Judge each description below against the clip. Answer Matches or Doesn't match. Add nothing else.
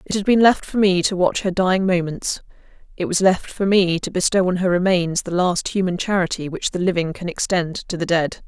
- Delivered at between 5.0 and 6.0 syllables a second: Matches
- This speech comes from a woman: Matches